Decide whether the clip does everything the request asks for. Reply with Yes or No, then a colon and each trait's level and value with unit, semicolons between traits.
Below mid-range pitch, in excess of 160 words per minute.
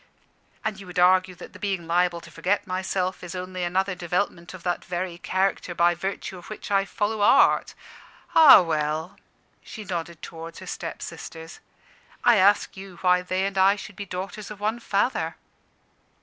No: medium, 185 Hz; average, 170 wpm